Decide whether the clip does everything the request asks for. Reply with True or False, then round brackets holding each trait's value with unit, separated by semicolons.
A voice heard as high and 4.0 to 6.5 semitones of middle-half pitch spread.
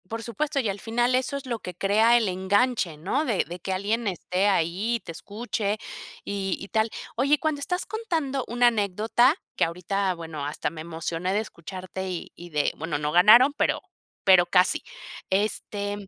True (200 Hz; 4.9 semitones)